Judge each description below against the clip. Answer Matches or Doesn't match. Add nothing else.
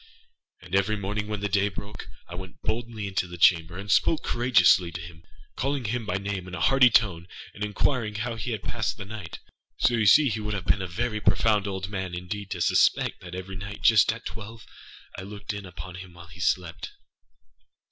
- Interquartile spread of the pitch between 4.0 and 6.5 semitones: Doesn't match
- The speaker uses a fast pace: Matches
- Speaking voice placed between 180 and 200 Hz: Doesn't match